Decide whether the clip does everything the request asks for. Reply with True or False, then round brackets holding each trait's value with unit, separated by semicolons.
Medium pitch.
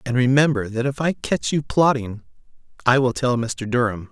False (125 Hz)